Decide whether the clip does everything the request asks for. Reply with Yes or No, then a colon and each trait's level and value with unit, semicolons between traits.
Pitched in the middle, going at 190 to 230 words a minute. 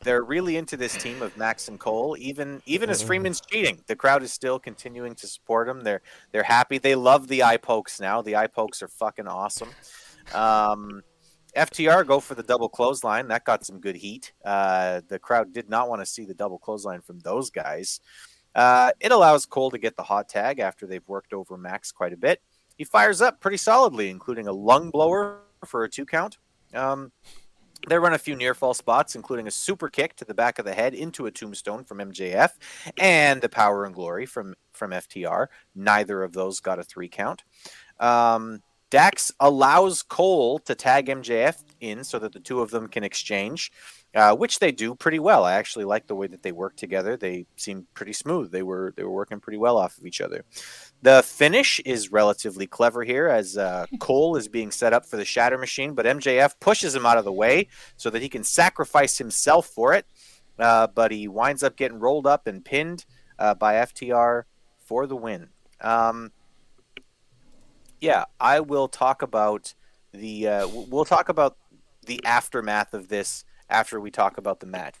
No: low, 120 Hz; average, 200 wpm